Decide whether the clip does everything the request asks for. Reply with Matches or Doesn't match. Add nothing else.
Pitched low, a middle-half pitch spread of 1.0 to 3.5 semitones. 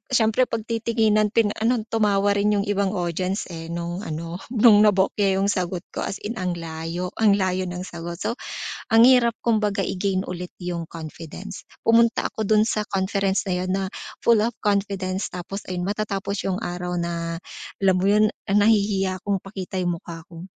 Doesn't match